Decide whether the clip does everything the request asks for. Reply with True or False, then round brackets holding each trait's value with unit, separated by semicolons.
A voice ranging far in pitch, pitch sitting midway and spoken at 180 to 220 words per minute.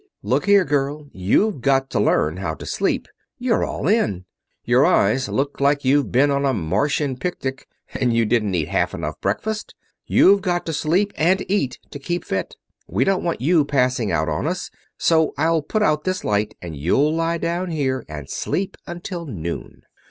True (6.9 semitones; 145 Hz; 185 wpm)